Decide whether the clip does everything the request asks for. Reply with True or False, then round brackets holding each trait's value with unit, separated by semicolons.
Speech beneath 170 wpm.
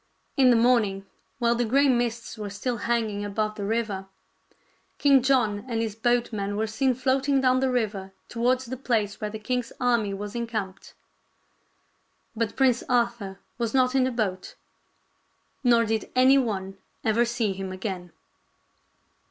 True (150 wpm)